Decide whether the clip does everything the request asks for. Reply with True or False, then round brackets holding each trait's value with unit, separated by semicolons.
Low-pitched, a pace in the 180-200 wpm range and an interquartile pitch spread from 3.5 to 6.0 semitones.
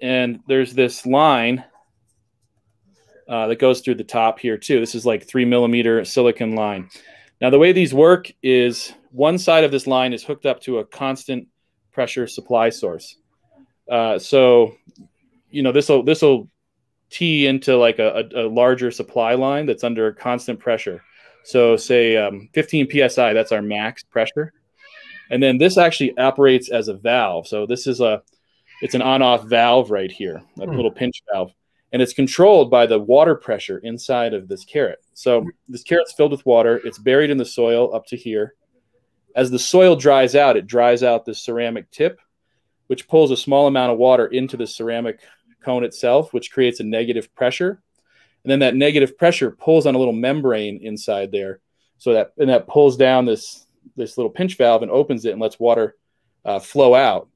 False (125 Hz; 185 wpm; 3.0 semitones)